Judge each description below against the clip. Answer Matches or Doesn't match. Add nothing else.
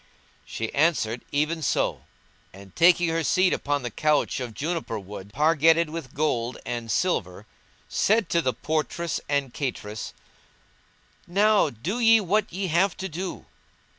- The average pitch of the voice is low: Doesn't match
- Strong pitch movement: Matches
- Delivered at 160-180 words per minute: Doesn't match